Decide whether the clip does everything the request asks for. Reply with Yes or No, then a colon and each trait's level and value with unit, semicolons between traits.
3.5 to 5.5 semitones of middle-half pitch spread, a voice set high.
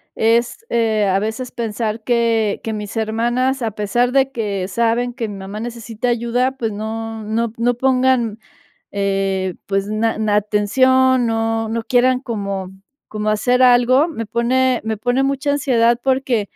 No: average, 2.7 semitones; high, 230 Hz